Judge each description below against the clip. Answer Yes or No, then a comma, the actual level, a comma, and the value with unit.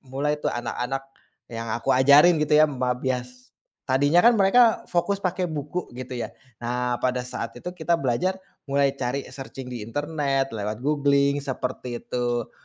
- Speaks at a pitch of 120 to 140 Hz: Yes, low, 135 Hz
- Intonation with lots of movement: No, average, 3.4 semitones